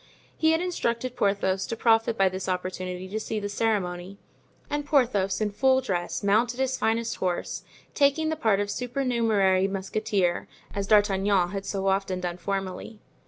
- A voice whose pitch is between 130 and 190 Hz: No, high, 205 Hz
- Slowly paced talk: No, average, 160 wpm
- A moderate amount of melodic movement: Yes, average, 3.6 semitones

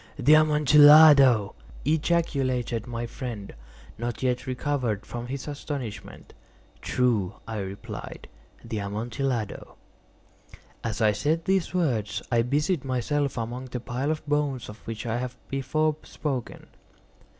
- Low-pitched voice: Yes, low, 125 Hz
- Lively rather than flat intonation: No, average, 4.1 semitones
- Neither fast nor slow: No, slow, 120 wpm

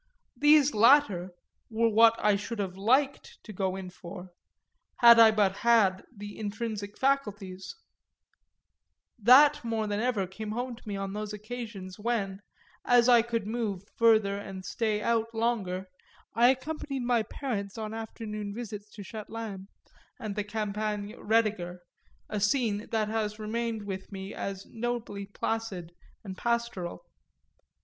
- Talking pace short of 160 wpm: Yes, average, 140 wpm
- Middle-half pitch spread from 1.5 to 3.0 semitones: Yes, average, 2.7 semitones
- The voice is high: Yes, high, 215 Hz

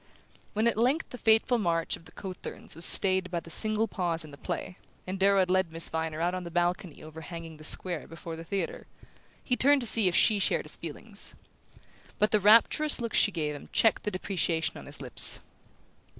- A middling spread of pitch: Yes, average, 4.4 semitones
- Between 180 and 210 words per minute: Yes, fast, 205 wpm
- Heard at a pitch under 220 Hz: Yes, medium, 185 Hz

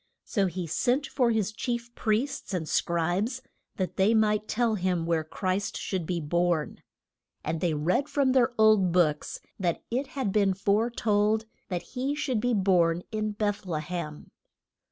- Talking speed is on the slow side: No, average, 165 wpm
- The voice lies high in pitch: Yes, high, 205 Hz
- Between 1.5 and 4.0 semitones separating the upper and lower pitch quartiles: No, average, 5.0 semitones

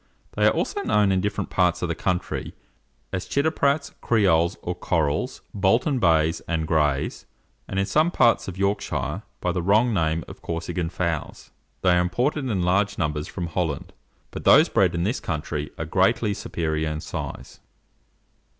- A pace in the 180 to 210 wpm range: No, average, 165 wpm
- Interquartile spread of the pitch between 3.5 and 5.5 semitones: Yes, average, 4.1 semitones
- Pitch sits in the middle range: No, very low, 90 Hz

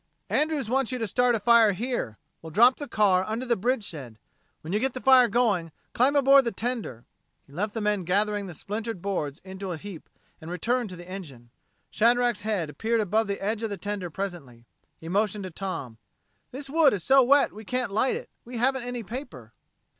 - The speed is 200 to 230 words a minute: Yes, fast, 205 wpm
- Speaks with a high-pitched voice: Yes, high, 210 Hz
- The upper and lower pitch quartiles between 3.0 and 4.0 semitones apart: No, average, 5.1 semitones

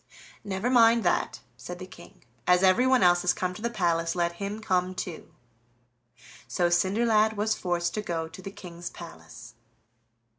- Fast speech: No, average, 160 wpm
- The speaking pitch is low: No, medium, 185 Hz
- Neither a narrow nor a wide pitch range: Yes, average, 3.5 semitones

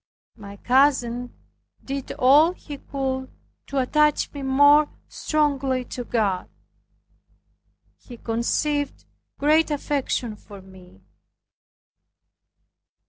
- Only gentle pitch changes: No, average, 3.5 semitones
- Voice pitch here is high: Yes, very high, 265 Hz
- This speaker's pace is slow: Yes, slow, 85 wpm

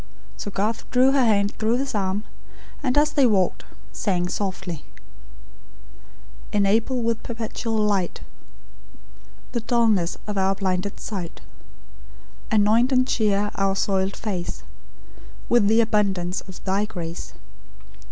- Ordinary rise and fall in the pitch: Yes, average, 3.2 semitones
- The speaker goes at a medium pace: No, slow, 120 wpm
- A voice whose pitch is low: No, high, 205 Hz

